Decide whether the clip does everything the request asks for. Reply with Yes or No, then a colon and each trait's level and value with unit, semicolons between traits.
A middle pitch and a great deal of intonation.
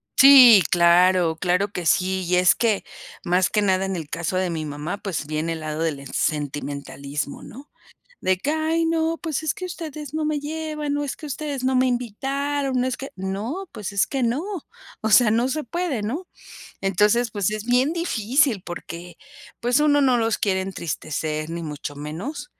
No: high, 215 Hz; wide, 8.4 semitones